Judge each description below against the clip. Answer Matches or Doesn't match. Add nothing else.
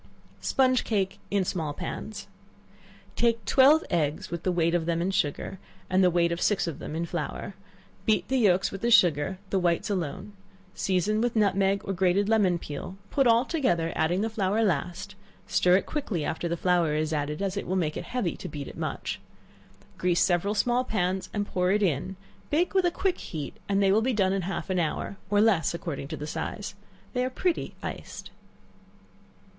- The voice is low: Doesn't match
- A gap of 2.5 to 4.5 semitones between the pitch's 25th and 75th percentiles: Matches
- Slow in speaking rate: Doesn't match